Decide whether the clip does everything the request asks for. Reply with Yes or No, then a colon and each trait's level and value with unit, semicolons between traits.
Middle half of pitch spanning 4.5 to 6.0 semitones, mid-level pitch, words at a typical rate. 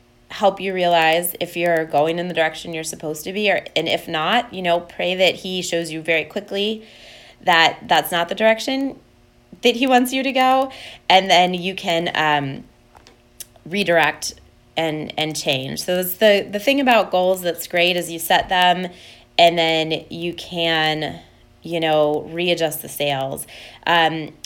No: average, 3.2 semitones; medium, 170 Hz; average, 170 wpm